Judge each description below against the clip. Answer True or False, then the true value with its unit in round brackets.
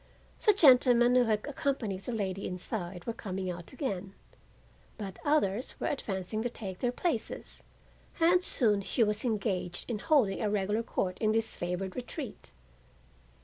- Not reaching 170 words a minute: True (150 wpm)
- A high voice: True (215 Hz)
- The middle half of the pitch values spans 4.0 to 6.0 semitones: True (4.4 semitones)